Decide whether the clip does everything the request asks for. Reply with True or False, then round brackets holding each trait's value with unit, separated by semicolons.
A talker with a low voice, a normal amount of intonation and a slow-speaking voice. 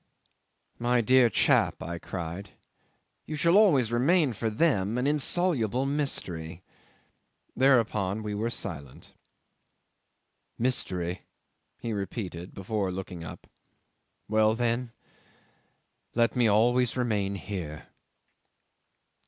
True (110 Hz; 4.7 semitones; 95 wpm)